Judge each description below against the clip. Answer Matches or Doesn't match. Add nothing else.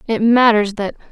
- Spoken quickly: Doesn't match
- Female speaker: Matches